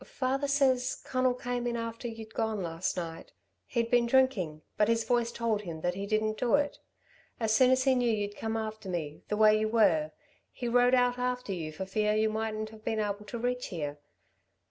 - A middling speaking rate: No, fast, 210 wpm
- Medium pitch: No, high, 220 Hz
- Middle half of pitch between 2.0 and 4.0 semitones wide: Yes, average, 3.2 semitones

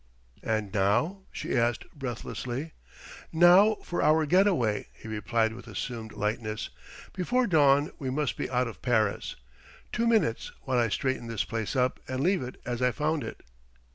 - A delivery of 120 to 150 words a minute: No, average, 165 wpm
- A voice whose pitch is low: Yes, low, 125 Hz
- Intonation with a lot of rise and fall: Yes, wide, 5.9 semitones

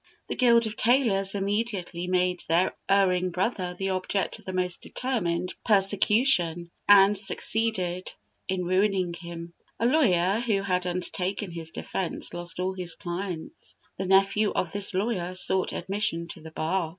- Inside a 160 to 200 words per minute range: No, average, 150 wpm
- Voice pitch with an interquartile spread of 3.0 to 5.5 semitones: No, narrow, 2.5 semitones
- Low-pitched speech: No, medium, 185 Hz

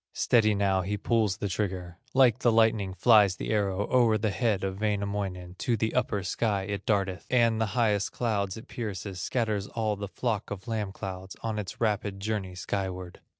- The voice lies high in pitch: No, low, 105 Hz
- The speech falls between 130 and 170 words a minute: No, average, 185 wpm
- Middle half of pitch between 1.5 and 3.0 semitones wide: Yes, narrow, 2.5 semitones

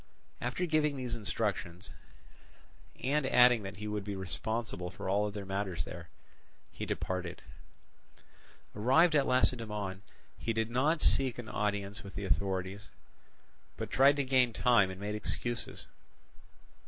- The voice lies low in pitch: Yes, low, 105 Hz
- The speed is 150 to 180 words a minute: No, slow, 135 wpm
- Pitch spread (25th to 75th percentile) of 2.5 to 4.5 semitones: Yes, average, 4.2 semitones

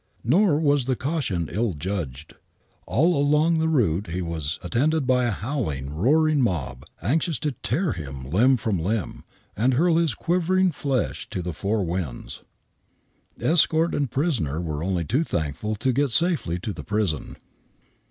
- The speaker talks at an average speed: Yes, average, 155 wpm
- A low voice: Yes, low, 115 Hz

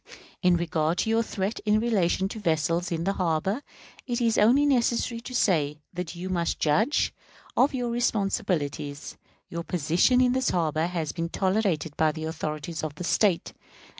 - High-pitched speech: No, medium, 180 Hz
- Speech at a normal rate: Yes, average, 165 wpm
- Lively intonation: Yes, wide, 5.7 semitones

